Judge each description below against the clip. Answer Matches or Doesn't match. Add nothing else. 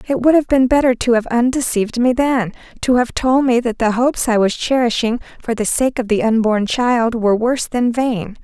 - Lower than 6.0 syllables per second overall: Matches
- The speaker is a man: Doesn't match